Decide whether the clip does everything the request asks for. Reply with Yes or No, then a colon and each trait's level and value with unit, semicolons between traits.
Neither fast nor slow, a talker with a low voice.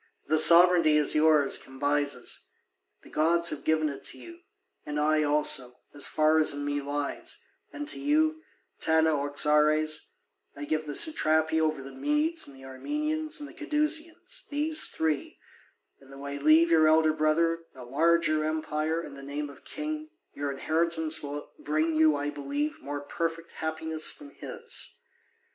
No: average, 155 wpm; medium, 155 Hz